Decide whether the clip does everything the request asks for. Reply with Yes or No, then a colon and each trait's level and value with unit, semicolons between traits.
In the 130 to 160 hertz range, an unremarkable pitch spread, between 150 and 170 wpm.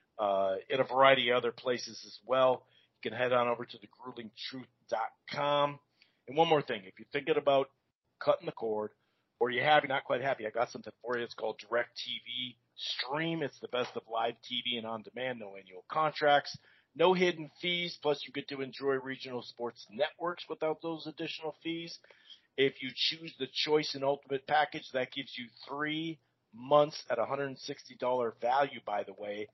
No: low, 135 Hz; average, 3.9 semitones; average, 185 wpm